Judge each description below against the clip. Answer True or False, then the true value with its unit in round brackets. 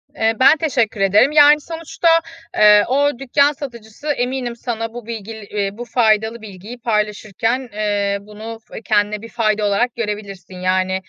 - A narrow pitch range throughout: False (3.1 semitones)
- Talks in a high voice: True (225 Hz)